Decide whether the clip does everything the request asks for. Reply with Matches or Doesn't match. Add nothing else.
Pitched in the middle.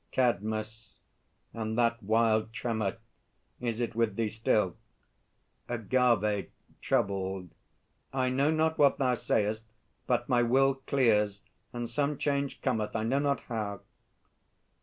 Doesn't match